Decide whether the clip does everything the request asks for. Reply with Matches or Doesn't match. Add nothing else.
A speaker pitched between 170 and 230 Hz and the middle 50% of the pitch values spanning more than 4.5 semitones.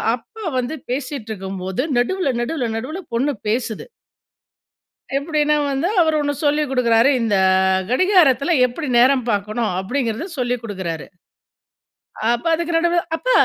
Doesn't match